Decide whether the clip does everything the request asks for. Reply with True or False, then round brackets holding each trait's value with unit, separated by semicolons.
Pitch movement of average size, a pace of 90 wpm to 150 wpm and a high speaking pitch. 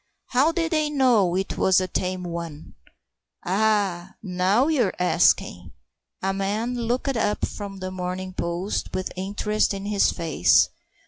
True (3.7 semitones; 140 wpm; 195 Hz)